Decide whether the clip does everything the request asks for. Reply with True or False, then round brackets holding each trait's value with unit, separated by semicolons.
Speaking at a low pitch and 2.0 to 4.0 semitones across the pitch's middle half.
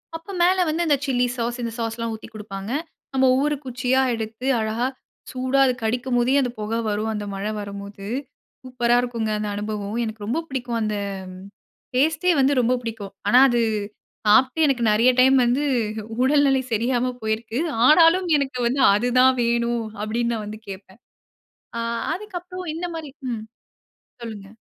False (240 Hz; 3.4 semitones)